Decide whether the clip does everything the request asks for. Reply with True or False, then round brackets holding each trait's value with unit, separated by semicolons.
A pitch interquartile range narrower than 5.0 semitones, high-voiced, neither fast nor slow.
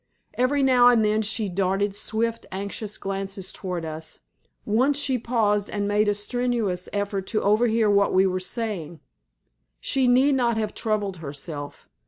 True (3.2 semitones; 210 Hz; 155 wpm)